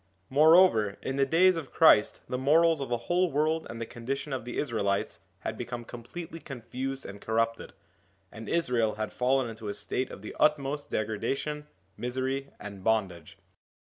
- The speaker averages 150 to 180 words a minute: Yes, average, 170 wpm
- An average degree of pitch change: Yes, average, 4.9 semitones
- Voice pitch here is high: No, low, 130 Hz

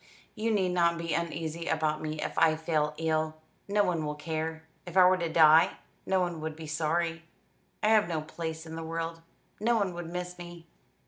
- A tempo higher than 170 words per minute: Yes, average, 200 wpm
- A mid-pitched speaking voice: Yes, medium, 165 Hz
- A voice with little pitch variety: Yes, narrow, 1.9 semitones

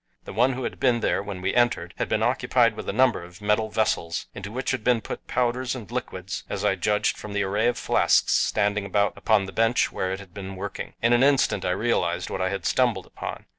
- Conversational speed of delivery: No, fast, 240 wpm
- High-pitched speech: No, low, 105 Hz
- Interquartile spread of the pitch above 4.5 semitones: No, average, 3.9 semitones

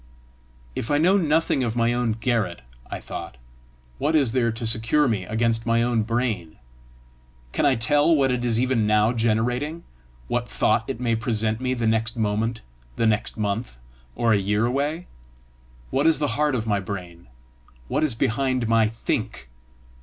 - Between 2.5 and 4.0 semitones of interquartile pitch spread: Yes, average, 2.9 semitones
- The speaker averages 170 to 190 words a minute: Yes, average, 175 wpm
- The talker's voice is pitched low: Yes, low, 115 Hz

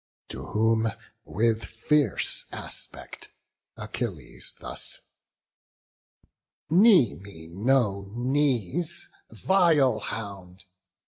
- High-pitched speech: No, low, 115 Hz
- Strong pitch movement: Yes, wide, 6.5 semitones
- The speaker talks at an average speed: No, slow, 70 wpm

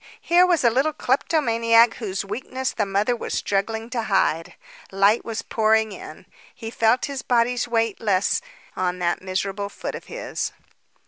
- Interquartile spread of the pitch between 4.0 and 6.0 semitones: No, average, 3.6 semitones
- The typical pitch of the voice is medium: No, high, 225 Hz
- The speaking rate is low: No, average, 155 wpm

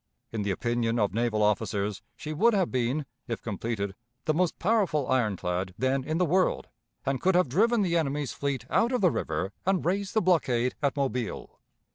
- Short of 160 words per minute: No, average, 185 wpm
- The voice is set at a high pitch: No, low, 135 Hz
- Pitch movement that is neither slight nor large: No, wide, 7.7 semitones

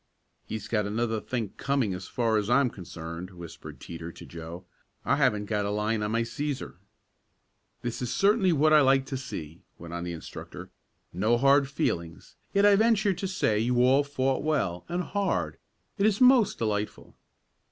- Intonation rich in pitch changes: Yes, wide, 6.3 semitones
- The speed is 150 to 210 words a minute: Yes, average, 175 wpm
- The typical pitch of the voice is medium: No, low, 120 Hz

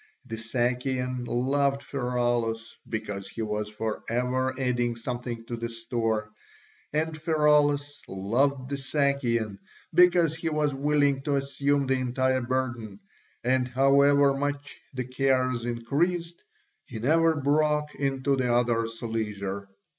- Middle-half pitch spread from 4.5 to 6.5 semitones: No, average, 3.3 semitones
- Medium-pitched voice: No, low, 130 Hz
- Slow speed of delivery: Yes, slow, 125 wpm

